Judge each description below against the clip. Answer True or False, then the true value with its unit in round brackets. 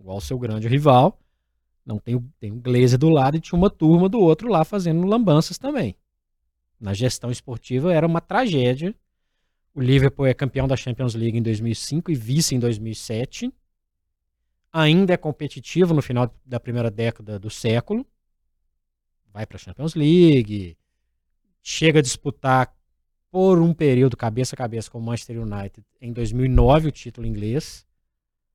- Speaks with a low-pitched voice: True (125 Hz)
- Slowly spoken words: False (155 wpm)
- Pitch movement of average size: False (6.3 semitones)